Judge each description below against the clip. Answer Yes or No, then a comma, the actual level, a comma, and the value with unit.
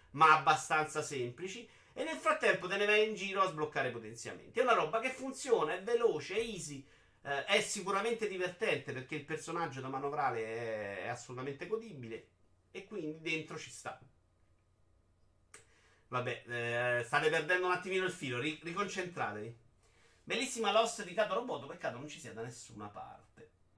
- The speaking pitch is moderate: Yes, medium, 155 Hz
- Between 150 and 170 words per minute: Yes, average, 155 wpm